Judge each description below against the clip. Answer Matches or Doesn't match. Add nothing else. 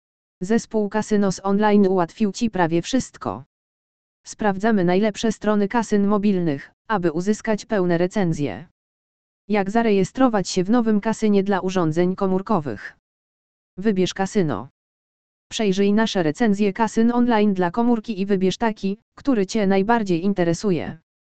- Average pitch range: Matches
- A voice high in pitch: Matches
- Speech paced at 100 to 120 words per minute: Matches